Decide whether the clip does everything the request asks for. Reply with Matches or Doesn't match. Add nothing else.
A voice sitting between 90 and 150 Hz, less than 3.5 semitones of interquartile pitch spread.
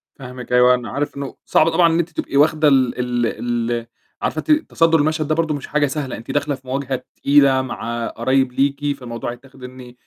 Matches